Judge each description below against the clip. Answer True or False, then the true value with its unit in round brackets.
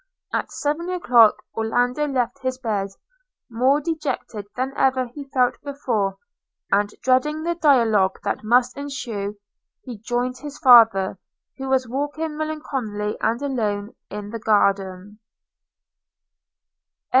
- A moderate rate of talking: False (120 wpm)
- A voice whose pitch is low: False (250 Hz)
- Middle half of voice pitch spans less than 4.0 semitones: False (4.8 semitones)